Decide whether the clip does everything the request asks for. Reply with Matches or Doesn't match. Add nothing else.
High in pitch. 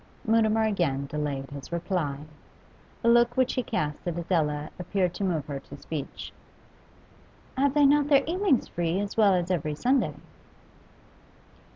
Doesn't match